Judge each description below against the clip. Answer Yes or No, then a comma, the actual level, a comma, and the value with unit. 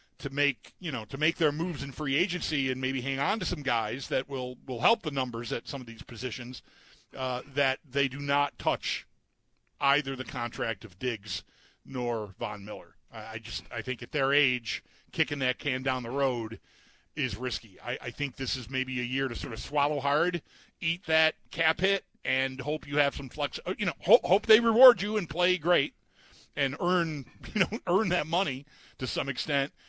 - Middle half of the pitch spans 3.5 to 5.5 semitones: Yes, average, 3.9 semitones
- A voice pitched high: No, medium, 140 Hz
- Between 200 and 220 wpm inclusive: Yes, fast, 205 wpm